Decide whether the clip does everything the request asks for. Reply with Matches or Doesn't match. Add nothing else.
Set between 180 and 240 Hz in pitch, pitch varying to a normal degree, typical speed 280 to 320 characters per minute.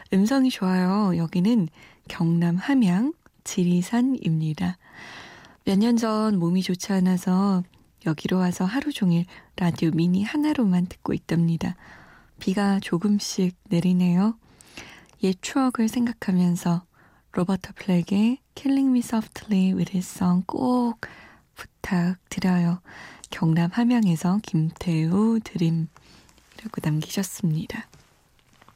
Doesn't match